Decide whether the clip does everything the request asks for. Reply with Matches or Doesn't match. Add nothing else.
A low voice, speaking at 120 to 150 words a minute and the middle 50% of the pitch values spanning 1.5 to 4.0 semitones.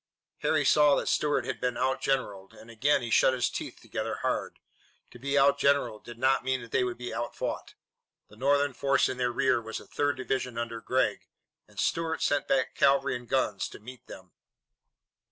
Doesn't match